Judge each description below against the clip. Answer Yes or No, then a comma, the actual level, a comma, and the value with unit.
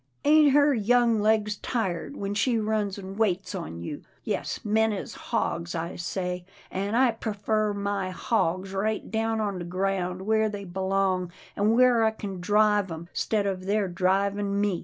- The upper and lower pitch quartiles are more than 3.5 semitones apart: No, average, 2.7 semitones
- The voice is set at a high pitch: Yes, high, 200 Hz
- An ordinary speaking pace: Yes, average, 170 wpm